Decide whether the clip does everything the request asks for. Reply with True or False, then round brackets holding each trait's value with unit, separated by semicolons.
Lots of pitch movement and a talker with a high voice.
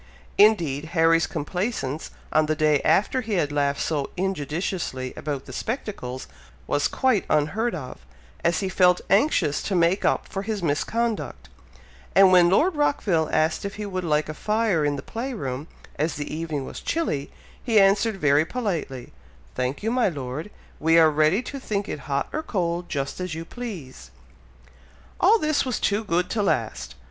False (6.2 semitones; 170 Hz)